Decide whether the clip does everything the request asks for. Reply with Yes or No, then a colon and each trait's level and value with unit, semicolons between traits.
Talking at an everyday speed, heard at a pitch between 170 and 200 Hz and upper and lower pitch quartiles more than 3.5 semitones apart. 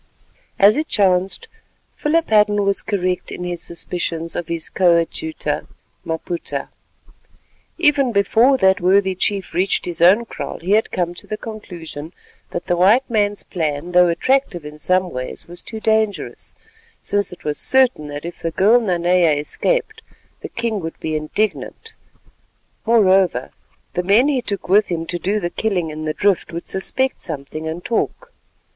Yes: average, 160 wpm; medium, 185 Hz; average, 4.2 semitones